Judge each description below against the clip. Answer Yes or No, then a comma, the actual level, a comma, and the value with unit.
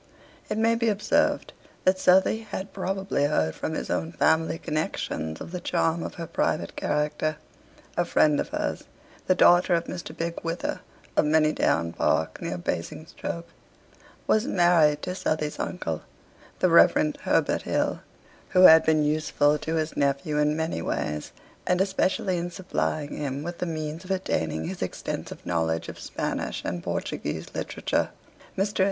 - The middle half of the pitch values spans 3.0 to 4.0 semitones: Yes, average, 3.6 semitones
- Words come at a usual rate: Yes, average, 155 wpm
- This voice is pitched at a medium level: Yes, medium, 160 Hz